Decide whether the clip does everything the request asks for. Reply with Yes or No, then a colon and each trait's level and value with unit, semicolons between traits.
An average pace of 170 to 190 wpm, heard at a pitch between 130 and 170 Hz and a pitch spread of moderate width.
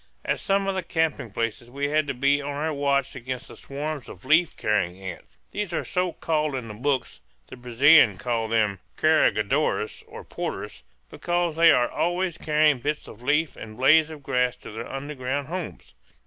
Yes: average, 185 wpm; medium, 140 Hz; average, 4.4 semitones